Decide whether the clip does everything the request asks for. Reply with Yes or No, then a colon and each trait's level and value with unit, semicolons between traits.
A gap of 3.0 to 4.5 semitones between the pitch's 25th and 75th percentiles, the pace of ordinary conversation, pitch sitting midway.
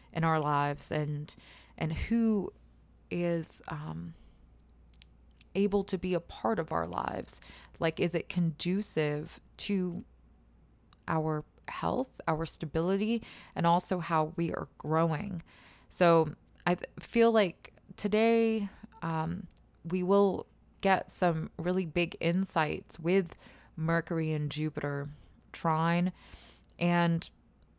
No: average, 3.8 semitones; slow, 110 wpm; medium, 165 Hz